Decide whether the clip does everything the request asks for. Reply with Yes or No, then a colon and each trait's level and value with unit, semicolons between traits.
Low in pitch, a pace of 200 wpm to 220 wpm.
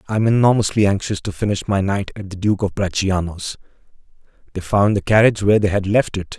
Yes: low, 100 Hz; fast, 205 wpm